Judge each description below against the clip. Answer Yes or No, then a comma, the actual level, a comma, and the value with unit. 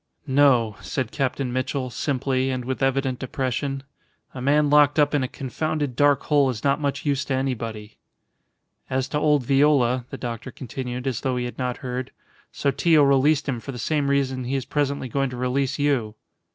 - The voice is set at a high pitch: No, low, 135 Hz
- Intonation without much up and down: Yes, narrow, 2.0 semitones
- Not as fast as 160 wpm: No, average, 185 wpm